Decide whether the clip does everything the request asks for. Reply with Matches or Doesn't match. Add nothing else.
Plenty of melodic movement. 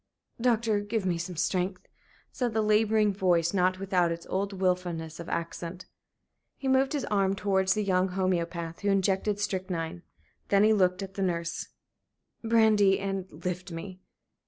Doesn't match